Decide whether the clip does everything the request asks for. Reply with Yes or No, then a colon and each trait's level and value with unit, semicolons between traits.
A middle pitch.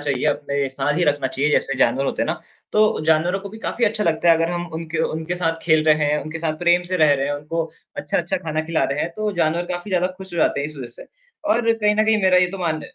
Yes: medium, 165 Hz